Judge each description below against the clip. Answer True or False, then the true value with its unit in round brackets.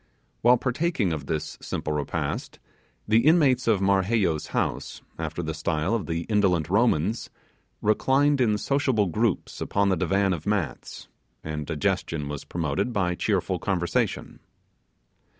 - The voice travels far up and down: True (6.1 semitones)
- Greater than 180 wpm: False (135 wpm)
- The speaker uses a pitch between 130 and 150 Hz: False (95 Hz)